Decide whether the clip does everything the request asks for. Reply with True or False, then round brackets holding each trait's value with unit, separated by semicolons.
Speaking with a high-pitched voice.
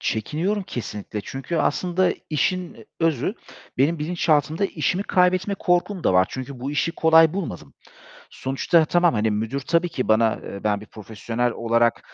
False (150 Hz)